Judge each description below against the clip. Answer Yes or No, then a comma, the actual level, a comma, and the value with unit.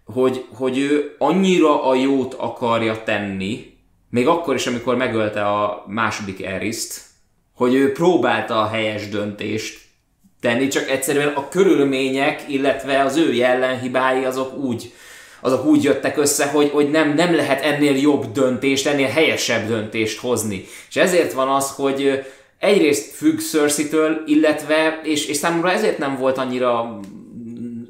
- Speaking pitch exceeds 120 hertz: Yes, low, 130 Hz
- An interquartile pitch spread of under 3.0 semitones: No, average, 4.2 semitones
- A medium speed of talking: Yes, average, 140 wpm